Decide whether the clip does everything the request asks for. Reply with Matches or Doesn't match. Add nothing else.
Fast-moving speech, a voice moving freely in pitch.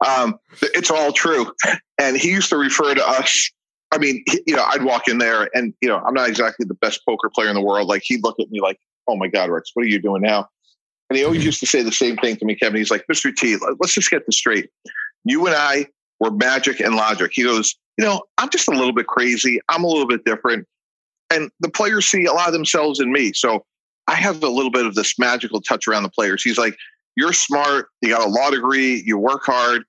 Matches